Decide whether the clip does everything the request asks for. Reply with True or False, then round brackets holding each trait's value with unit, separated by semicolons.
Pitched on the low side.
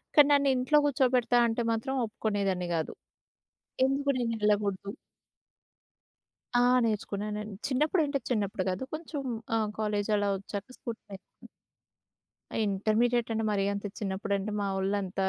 False (215 Hz)